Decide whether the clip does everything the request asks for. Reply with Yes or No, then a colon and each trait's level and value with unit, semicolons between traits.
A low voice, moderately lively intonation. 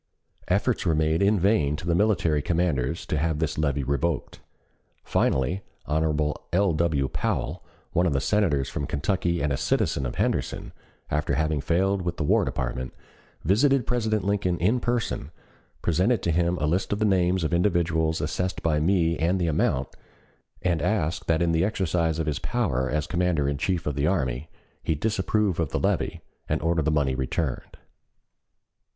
Yes: very low, 85 Hz; average, 3.9 semitones